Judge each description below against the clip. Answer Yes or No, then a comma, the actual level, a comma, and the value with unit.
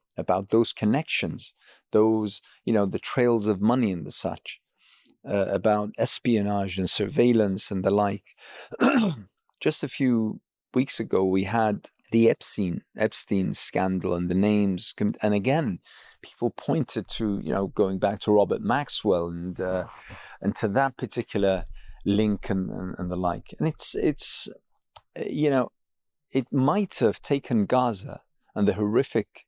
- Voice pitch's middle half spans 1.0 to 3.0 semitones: No, average, 4.0 semitones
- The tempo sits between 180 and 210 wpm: No, average, 145 wpm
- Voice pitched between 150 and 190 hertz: No, low, 105 Hz